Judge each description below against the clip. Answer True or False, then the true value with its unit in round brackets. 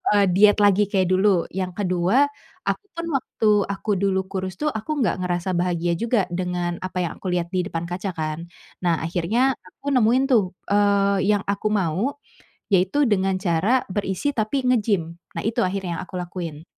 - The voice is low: False (190 Hz)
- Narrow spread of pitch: False (3.1 semitones)